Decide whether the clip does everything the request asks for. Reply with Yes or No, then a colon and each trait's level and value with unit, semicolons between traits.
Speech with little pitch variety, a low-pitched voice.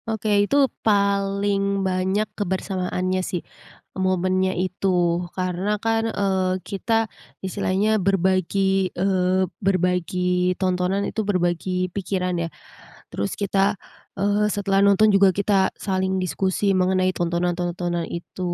No: narrow, 1.5 semitones; high, 190 Hz